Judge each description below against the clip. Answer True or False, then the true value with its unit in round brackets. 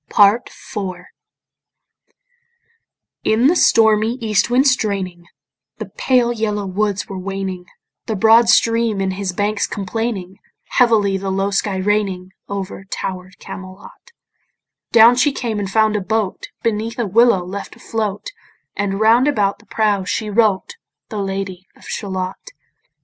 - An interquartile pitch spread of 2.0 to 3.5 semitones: True (2.7 semitones)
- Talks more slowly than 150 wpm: True (135 wpm)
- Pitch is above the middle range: True (205 Hz)